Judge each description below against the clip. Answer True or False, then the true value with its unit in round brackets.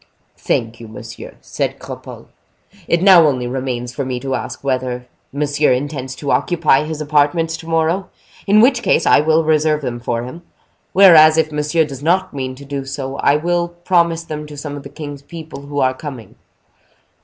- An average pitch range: True (3.5 semitones)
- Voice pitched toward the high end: False (150 Hz)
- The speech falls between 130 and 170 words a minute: False (185 wpm)